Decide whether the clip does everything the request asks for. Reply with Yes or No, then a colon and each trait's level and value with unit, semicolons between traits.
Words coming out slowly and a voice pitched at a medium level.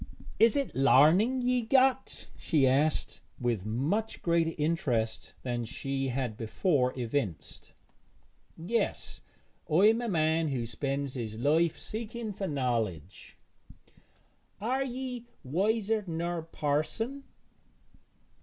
Yes: slow, 105 wpm; medium, 160 Hz